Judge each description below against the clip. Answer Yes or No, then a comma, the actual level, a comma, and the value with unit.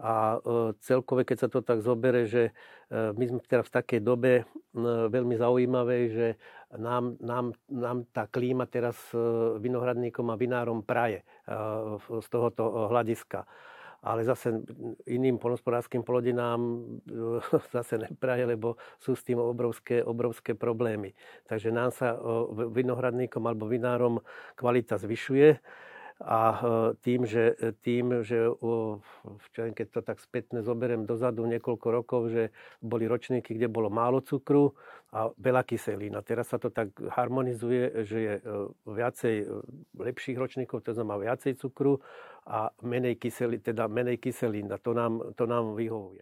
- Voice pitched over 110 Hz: Yes, low, 120 Hz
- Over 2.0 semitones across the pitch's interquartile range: No, narrow, 1.4 semitones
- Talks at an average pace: Yes, average, 130 wpm